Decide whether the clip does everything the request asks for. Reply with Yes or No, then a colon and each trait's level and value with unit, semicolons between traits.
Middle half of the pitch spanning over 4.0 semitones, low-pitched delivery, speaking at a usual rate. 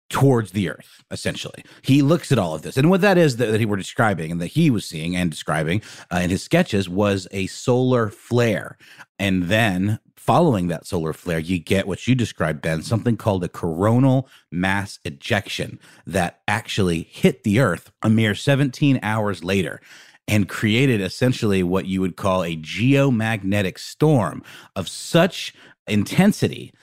Yes: wide, 5.6 semitones; low, 105 Hz; average, 170 wpm